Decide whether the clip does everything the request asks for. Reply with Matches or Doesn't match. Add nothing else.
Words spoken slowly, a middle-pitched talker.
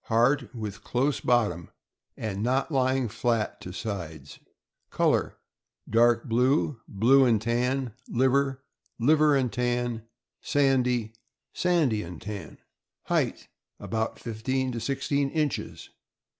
Doesn't match